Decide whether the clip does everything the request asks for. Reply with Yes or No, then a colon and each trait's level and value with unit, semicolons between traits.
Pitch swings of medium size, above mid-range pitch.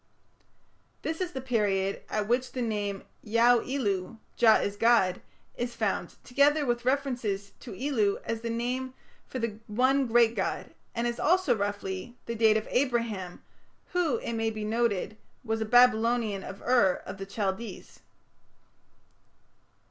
Yes: average, 3.2 semitones; high, 230 Hz